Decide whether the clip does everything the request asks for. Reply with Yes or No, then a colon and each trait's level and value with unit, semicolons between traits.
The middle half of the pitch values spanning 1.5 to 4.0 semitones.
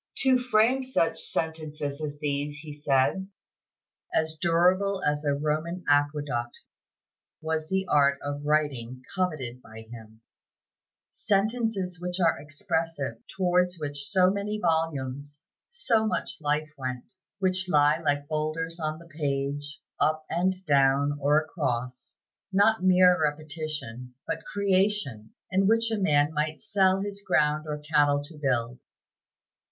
No: average, 4.4 semitones